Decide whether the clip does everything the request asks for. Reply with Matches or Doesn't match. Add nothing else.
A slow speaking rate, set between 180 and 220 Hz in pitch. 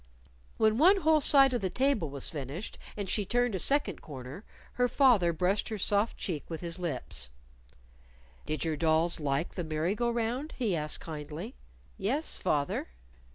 Doesn't match